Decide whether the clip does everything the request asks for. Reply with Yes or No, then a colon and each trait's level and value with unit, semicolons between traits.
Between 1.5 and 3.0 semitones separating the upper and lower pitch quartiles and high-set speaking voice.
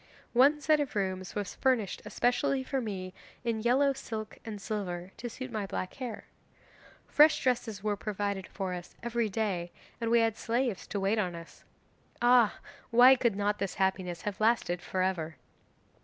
No: average, 4.1 semitones; high, 215 Hz